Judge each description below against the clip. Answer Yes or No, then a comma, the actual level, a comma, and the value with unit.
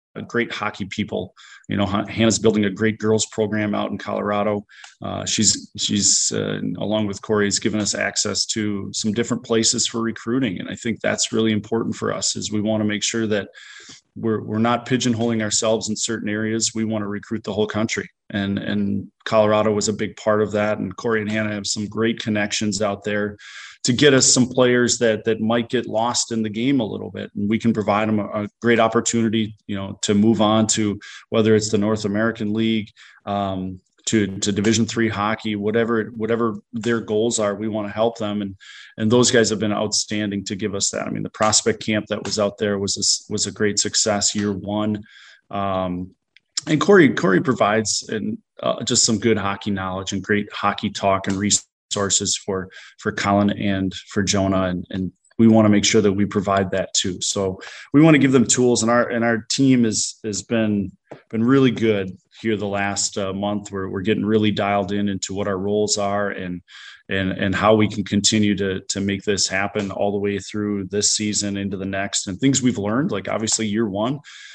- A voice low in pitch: Yes, low, 105 Hz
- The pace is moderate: No, fast, 210 wpm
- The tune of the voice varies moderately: No, narrow, 1.8 semitones